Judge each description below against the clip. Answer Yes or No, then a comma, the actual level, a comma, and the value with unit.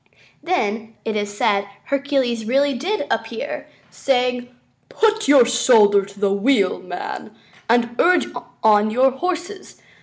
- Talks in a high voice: Yes, high, 245 Hz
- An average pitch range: Yes, average, 4.9 semitones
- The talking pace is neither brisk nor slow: No, slow, 125 wpm